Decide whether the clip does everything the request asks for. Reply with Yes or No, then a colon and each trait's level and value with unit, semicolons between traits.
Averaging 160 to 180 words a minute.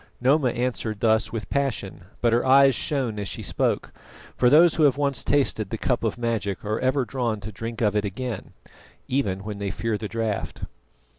No: average, 195 wpm